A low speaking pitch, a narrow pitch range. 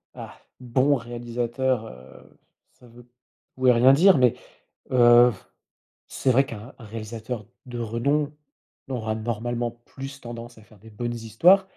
Yes: low, 120 Hz; narrow, 2.2 semitones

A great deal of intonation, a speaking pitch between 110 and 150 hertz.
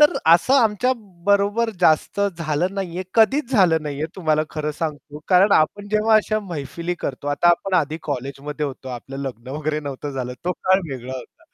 No: wide, 5.7 semitones; medium, 165 Hz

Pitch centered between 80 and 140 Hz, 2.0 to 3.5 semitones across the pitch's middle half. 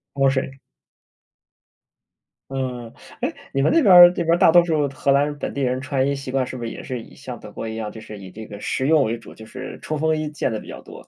No: low, 135 Hz; average, 4.3 semitones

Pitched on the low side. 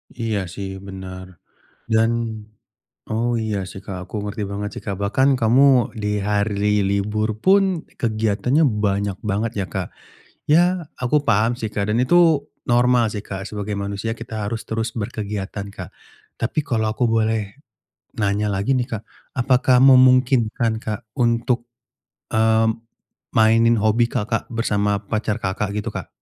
Yes: low, 110 Hz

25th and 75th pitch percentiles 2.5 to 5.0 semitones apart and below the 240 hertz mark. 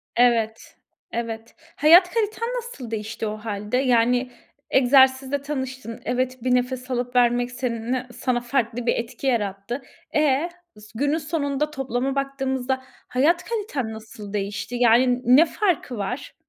No: average, 2.9 semitones; very high, 250 Hz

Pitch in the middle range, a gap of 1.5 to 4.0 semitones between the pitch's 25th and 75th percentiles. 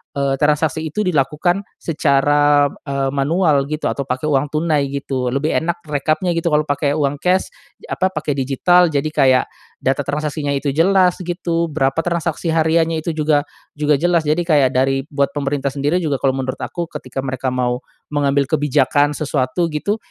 Yes: medium, 150 Hz; average, 3.0 semitones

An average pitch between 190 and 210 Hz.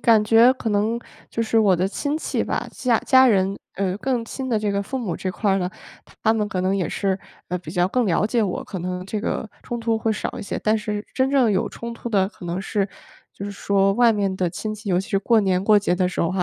Yes: high, 205 Hz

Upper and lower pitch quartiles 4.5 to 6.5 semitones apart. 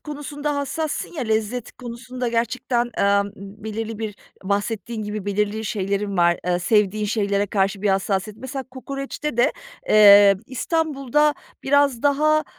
Yes: average, 4.8 semitones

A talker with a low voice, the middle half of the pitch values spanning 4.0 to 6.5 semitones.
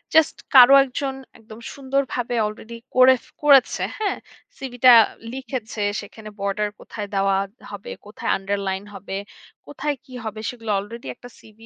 No: high, 230 Hz; average, 4.3 semitones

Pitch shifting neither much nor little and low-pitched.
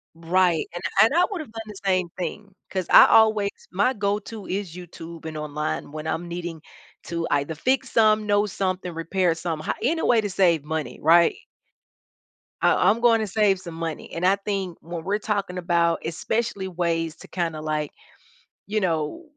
No: average, 3.9 semitones; medium, 180 Hz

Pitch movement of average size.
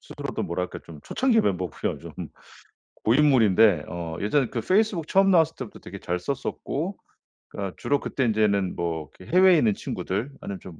No: wide, 8.7 semitones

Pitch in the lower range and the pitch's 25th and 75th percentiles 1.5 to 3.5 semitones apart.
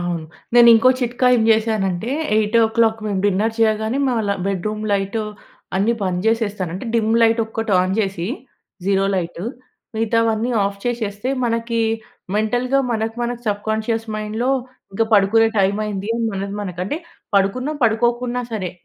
No: high, 220 Hz; narrow, 2.6 semitones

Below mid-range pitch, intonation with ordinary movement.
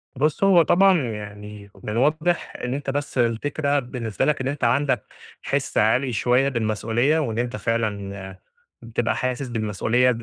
Yes: low, 120 Hz; average, 4.3 semitones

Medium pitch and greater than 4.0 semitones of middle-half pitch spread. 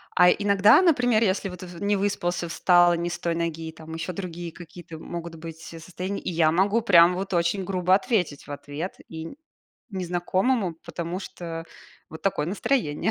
No: medium, 175 Hz; average, 2.8 semitones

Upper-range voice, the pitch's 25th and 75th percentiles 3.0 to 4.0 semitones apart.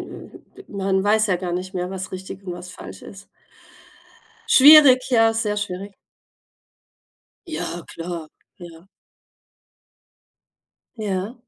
Yes: high, 195 Hz; average, 3.4 semitones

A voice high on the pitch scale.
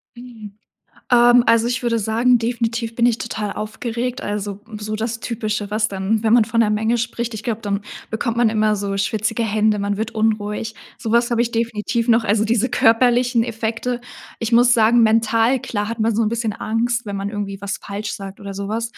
Yes: high, 225 Hz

